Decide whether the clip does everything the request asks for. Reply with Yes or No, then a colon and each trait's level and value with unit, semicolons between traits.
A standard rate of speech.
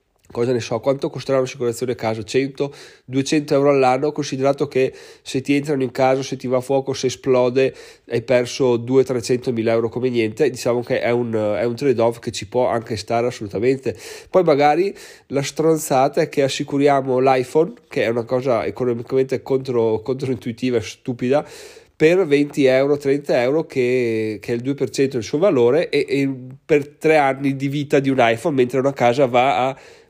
No: fast, 180 wpm